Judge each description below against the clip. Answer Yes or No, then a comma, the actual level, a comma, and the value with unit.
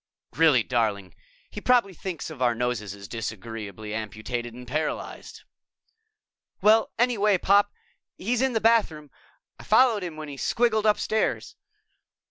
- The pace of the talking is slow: Yes, slow, 130 wpm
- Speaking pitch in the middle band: Yes, medium, 155 Hz